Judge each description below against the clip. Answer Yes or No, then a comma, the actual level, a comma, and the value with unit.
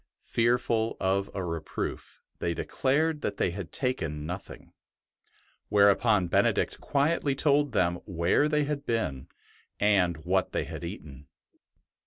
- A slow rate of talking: Yes, slow, 130 wpm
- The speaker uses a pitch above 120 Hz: No, low, 100 Hz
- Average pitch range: No, wide, 8.1 semitones